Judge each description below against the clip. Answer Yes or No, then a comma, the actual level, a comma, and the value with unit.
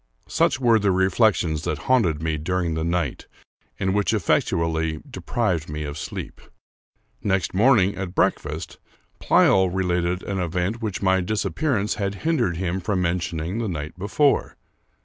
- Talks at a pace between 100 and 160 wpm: Yes, average, 150 wpm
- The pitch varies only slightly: No, average, 3.6 semitones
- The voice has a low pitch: Yes, very low, 90 Hz